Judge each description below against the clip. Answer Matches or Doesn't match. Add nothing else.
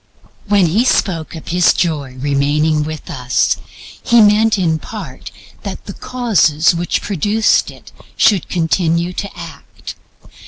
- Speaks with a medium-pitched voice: Matches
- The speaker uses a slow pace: Matches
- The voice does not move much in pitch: Doesn't match